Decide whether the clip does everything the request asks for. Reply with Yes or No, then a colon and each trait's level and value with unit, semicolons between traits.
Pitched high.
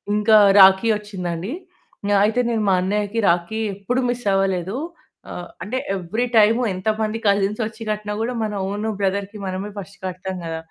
Yes: high, 205 Hz